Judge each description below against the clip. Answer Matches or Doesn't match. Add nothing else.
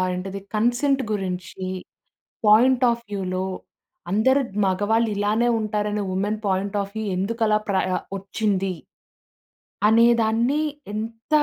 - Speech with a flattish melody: Doesn't match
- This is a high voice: Matches